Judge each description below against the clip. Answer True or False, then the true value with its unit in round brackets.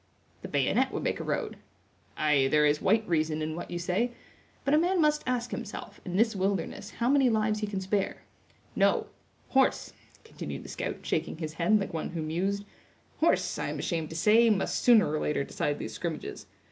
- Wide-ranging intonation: True (6.1 semitones)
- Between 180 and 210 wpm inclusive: True (195 wpm)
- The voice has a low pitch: False (190 Hz)